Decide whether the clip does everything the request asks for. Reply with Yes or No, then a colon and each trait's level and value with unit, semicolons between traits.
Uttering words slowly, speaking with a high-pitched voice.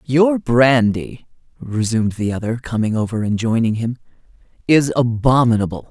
No: slow, 120 wpm; low, 120 Hz